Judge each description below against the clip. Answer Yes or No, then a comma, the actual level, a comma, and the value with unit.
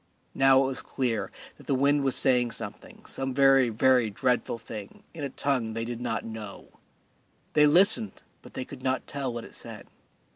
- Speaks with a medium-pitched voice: No, low, 130 Hz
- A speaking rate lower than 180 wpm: No, average, 190 wpm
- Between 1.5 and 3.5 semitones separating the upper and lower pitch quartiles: Yes, average, 2.9 semitones